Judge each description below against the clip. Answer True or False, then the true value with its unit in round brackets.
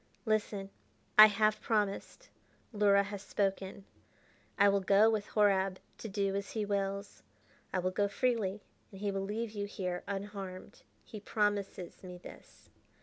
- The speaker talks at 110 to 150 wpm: True (145 wpm)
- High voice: True (200 Hz)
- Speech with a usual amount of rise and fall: False (1.4 semitones)